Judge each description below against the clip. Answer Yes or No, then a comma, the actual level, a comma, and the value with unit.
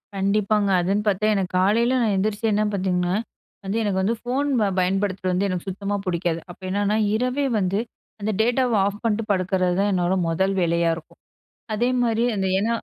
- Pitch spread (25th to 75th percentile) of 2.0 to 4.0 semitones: Yes, average, 2.8 semitones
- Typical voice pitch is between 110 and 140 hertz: No, high, 200 Hz